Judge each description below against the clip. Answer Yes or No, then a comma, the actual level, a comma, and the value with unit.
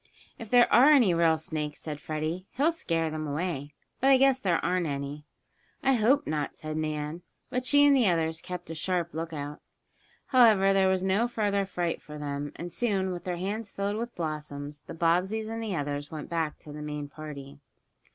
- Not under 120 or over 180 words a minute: No, average, 195 wpm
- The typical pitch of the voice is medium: Yes, medium, 170 Hz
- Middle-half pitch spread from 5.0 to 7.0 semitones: Yes, wide, 5.4 semitones